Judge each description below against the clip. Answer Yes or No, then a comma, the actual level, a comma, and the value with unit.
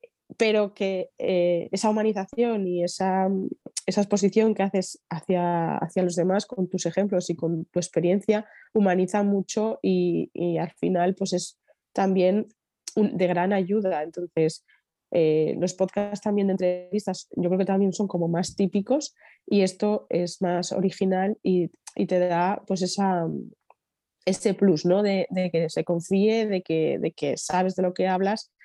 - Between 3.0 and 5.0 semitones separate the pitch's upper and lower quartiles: No, narrow, 2.5 semitones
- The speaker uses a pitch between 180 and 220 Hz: Yes, high, 190 Hz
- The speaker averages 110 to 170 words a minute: Yes, average, 165 wpm